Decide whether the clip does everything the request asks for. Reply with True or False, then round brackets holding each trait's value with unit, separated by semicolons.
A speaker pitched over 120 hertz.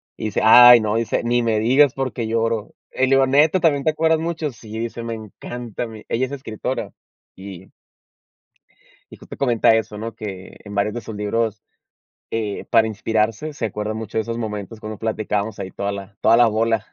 False (115 Hz)